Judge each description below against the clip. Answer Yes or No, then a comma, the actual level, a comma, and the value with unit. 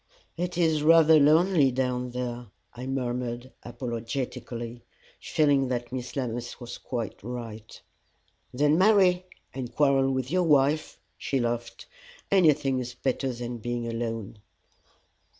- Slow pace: Yes, slow, 120 wpm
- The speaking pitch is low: Yes, low, 130 Hz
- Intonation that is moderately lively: Yes, average, 3.7 semitones